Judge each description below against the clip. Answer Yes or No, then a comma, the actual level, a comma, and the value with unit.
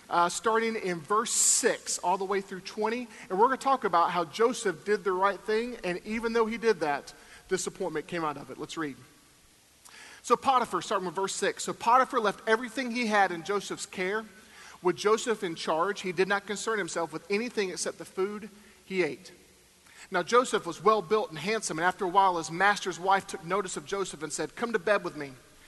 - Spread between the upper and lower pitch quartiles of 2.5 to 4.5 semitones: Yes, average, 3.6 semitones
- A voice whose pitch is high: Yes, high, 200 Hz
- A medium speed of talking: No, fast, 215 wpm